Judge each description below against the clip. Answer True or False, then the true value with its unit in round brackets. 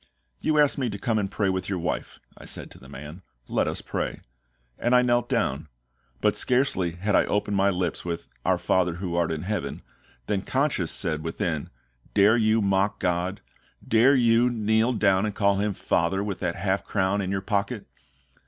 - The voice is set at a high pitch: False (100 Hz)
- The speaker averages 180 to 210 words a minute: True (190 wpm)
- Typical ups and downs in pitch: True (3.6 semitones)